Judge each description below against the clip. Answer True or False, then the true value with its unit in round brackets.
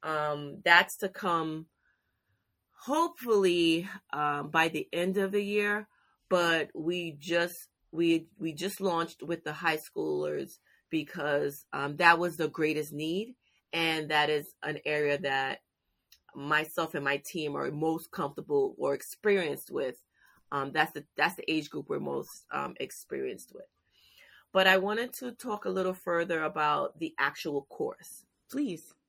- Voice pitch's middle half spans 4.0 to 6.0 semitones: True (4.5 semitones)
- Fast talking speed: False (145 wpm)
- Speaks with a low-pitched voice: False (170 Hz)